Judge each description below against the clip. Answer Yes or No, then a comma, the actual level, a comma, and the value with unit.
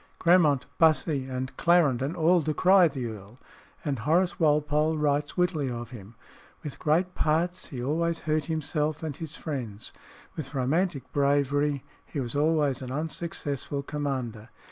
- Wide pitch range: No, average, 3.4 semitones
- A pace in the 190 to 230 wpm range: No, average, 140 wpm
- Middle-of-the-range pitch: Yes, medium, 150 Hz